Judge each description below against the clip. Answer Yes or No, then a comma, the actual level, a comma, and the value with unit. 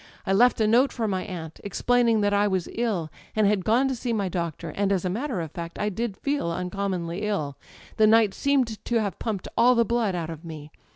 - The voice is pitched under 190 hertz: No, high, 205 Hz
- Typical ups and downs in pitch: Yes, average, 4.5 semitones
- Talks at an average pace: No, fast, 235 wpm